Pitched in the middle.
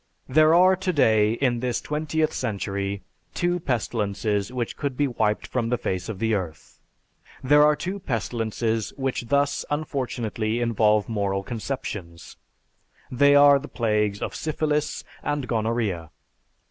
No: low, 120 Hz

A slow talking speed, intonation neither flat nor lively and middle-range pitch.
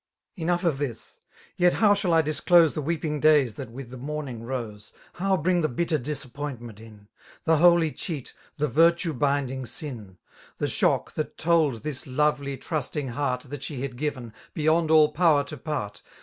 No: average, 175 wpm; average, 4.1 semitones; medium, 145 Hz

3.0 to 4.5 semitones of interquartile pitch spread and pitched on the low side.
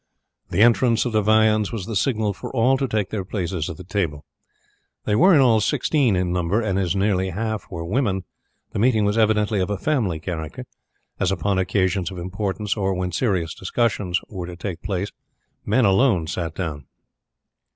Yes: average, 3.3 semitones; low, 100 Hz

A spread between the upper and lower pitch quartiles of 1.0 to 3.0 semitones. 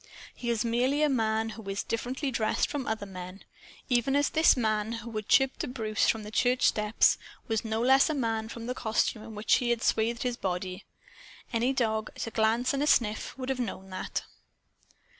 Yes: narrow, 2.6 semitones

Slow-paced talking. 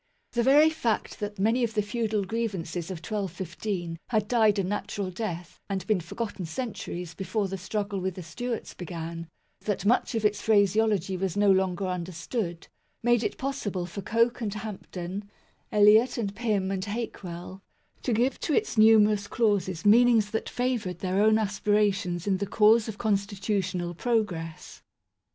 No: average, 160 wpm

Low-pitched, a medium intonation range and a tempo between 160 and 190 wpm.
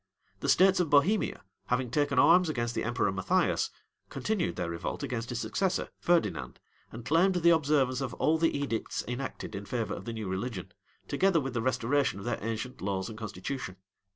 No: low, 125 Hz; wide, 6.1 semitones; average, 180 wpm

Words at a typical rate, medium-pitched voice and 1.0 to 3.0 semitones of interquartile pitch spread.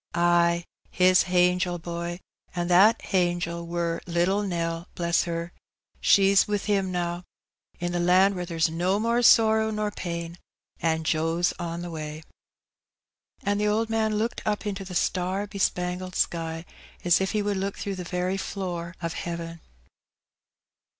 Yes: average, 150 wpm; medium, 180 Hz; narrow, 2.5 semitones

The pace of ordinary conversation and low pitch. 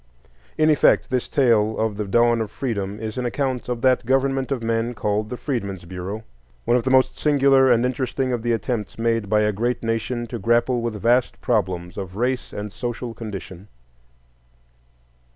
Yes: average, 175 wpm; low, 115 Hz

